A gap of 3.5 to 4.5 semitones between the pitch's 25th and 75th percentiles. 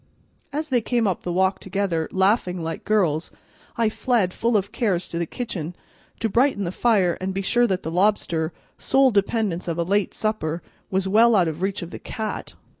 Yes: average, 4.1 semitones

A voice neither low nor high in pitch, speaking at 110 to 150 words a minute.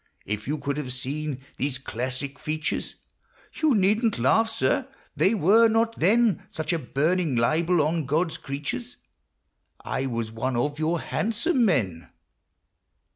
Yes: medium, 155 Hz; average, 140 wpm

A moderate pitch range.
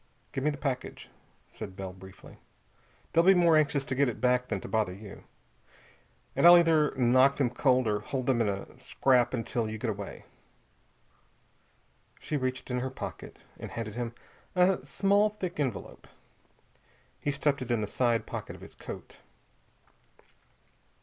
Yes: average, 4.4 semitones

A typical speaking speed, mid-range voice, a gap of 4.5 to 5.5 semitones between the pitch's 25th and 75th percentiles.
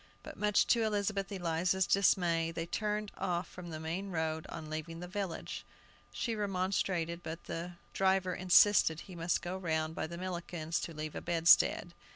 No: average, 165 wpm; medium, 175 Hz; average, 2.7 semitones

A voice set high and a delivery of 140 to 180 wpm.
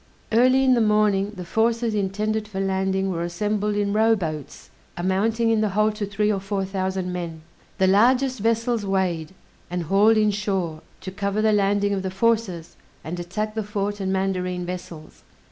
Yes: high, 200 Hz; average, 175 wpm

